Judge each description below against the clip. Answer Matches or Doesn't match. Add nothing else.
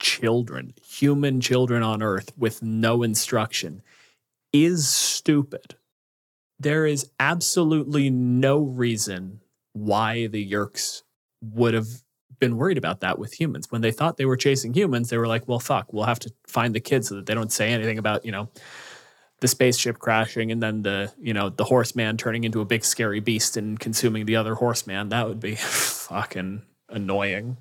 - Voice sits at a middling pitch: Doesn't match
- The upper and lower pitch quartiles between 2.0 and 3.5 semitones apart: Matches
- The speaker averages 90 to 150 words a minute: Doesn't match